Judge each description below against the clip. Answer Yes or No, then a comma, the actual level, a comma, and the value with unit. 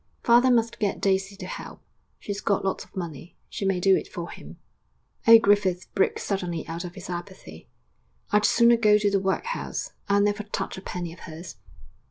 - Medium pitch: No, high, 195 Hz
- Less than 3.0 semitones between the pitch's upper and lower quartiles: Yes, narrow, 2.6 semitones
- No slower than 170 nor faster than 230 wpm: Yes, average, 190 wpm